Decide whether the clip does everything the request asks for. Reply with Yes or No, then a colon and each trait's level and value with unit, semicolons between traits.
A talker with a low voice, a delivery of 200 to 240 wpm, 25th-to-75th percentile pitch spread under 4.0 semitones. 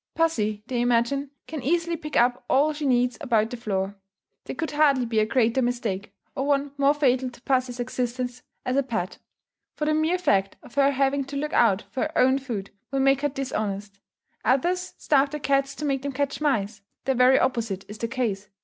No: very high, 260 Hz; fast, 205 wpm; average, 3.4 semitones